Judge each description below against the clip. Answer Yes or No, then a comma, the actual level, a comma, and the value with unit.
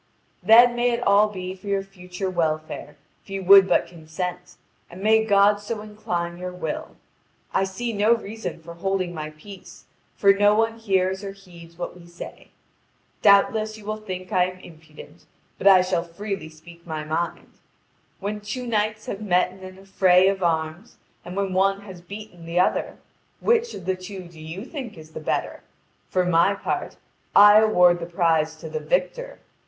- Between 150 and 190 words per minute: Yes, average, 180 wpm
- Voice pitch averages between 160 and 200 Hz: Yes, high, 190 Hz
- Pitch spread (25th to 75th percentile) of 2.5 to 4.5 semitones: Yes, average, 3.2 semitones